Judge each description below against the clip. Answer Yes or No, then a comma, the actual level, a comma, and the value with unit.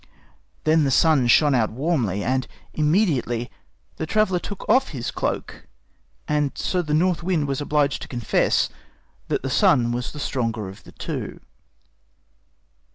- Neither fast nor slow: Yes, average, 150 wpm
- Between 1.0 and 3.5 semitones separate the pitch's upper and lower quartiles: No, average, 5.1 semitones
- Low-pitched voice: No, medium, 145 Hz